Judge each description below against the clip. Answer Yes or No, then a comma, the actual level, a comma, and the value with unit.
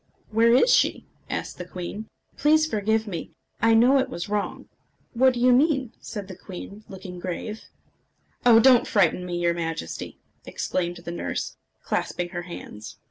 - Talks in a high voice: Yes, high, 205 Hz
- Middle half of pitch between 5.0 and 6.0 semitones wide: Yes, wide, 5.5 semitones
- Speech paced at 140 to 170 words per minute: Yes, average, 160 wpm